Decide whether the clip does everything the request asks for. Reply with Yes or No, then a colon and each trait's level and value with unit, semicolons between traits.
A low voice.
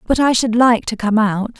No: high, 230 Hz